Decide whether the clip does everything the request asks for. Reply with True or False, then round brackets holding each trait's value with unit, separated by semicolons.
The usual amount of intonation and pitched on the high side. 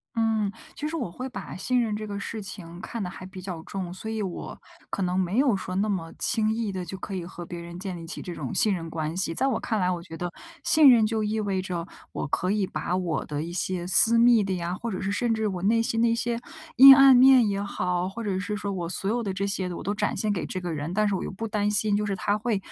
True (3.6 semitones; 200 Hz)